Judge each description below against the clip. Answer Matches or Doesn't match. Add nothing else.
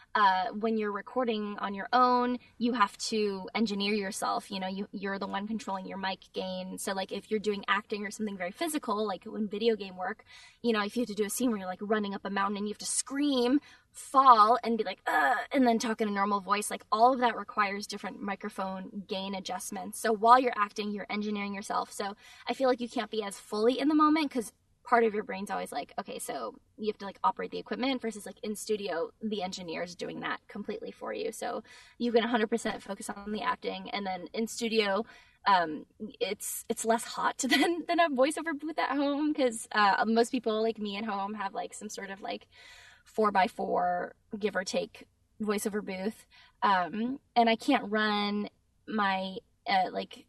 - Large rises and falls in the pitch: Doesn't match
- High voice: Matches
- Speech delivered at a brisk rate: Matches